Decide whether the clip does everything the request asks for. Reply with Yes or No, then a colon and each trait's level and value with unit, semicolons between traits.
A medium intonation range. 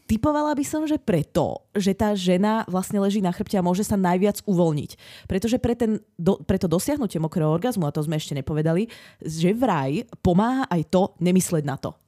Yes: average, 4.3 semitones